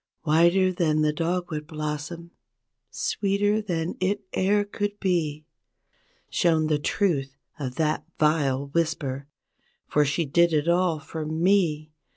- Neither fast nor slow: No, slow, 125 wpm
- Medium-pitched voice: Yes, medium, 160 Hz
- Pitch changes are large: No, average, 3.2 semitones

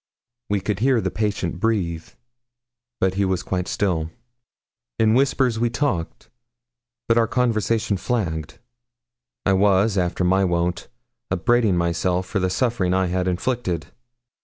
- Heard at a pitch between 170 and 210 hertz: No, very low, 95 Hz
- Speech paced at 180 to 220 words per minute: No, slow, 135 wpm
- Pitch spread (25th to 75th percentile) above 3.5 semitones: Yes, average, 4.1 semitones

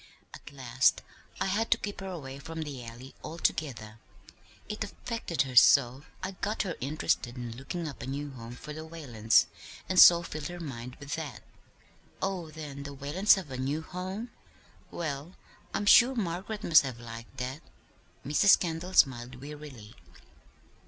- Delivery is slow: No, average, 160 wpm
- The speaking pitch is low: No, medium, 150 Hz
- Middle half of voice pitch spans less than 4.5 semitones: No, average, 5.3 semitones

